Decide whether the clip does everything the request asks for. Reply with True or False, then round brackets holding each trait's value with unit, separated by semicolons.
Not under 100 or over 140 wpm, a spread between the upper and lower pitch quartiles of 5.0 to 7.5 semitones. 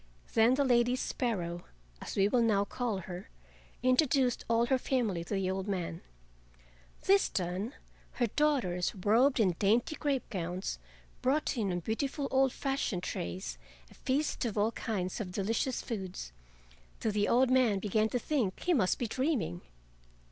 False (155 wpm; 5.4 semitones)